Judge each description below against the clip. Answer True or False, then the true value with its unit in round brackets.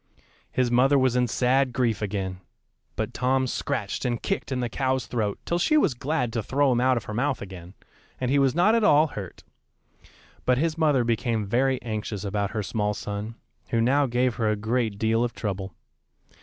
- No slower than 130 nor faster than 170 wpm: False (195 wpm)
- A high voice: False (120 Hz)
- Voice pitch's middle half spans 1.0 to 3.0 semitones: False (3.7 semitones)